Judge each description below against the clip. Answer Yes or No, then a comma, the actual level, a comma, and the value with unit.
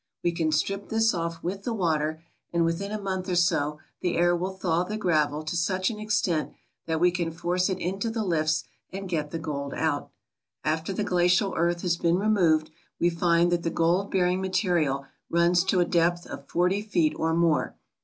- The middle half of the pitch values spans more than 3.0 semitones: No, narrow, 2.4 semitones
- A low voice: No, medium, 175 Hz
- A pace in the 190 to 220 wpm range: Yes, average, 200 wpm